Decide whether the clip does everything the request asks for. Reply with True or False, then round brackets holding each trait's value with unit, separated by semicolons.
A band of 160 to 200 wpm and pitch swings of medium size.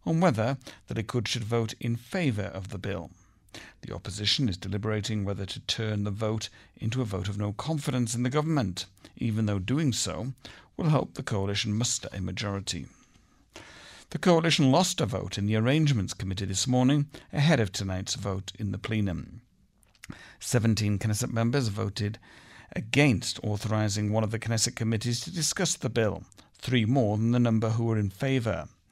True (170 wpm; 4.2 semitones)